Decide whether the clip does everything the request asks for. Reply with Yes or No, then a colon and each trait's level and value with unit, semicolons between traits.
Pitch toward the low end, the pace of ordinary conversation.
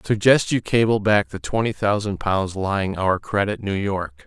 Yes: low, 100 Hz; average, 185 wpm